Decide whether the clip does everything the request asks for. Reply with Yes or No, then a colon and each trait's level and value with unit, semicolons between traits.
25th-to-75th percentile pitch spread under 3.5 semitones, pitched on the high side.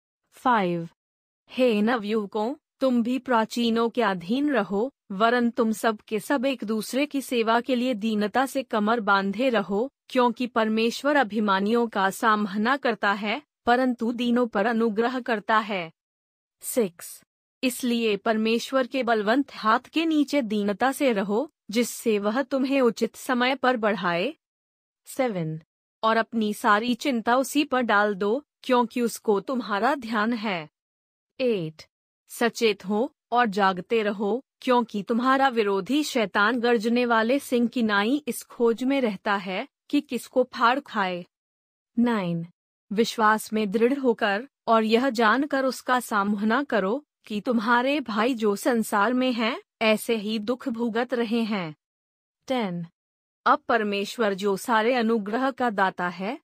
Yes: average, 3.1 semitones; high, 230 Hz